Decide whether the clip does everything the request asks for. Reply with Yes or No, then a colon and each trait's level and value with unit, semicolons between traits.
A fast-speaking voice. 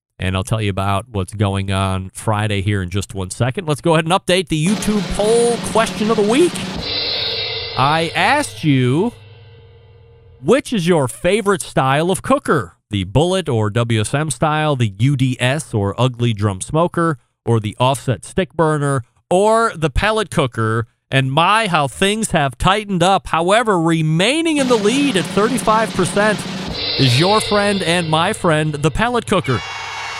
No: average, 155 wpm